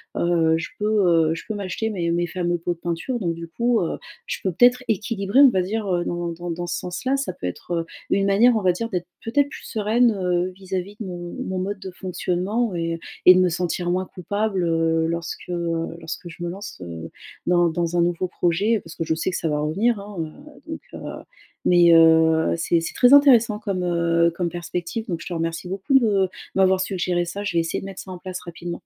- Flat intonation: No, average, 3.1 semitones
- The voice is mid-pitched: Yes, medium, 180 Hz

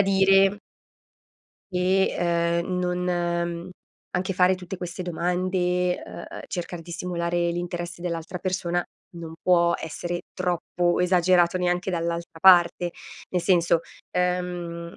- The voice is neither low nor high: Yes, medium, 175 Hz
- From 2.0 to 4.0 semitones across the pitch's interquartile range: No, narrow, 0.9 semitones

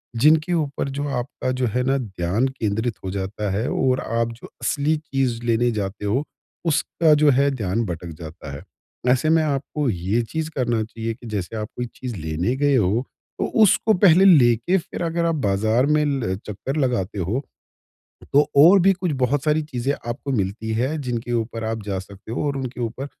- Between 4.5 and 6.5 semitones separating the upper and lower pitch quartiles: Yes, average, 5.0 semitones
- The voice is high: No, low, 125 Hz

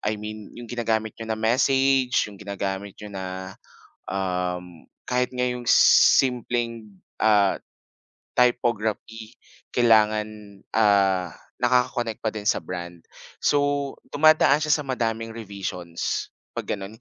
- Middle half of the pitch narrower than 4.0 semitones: Yes, average, 3.6 semitones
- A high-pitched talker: No, low, 110 Hz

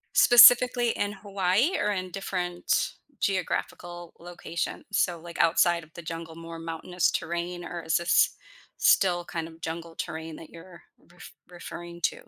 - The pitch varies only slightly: Yes, narrow, 1.8 semitones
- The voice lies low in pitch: No, medium, 175 Hz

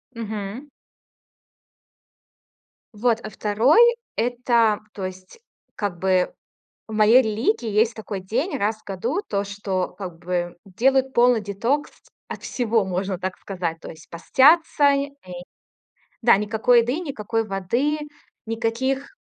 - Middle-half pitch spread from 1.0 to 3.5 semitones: No, average, 4.2 semitones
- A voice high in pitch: Yes, high, 220 Hz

